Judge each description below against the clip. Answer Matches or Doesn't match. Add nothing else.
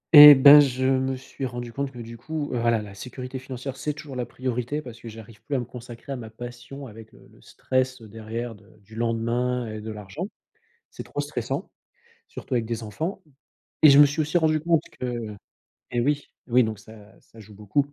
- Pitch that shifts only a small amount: Doesn't match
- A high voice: Doesn't match